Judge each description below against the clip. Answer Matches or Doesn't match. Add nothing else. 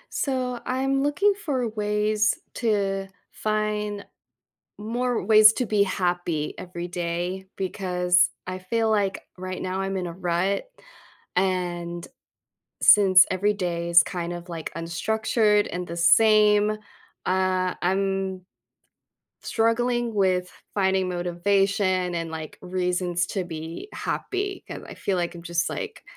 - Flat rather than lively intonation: Doesn't match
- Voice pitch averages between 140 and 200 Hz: Matches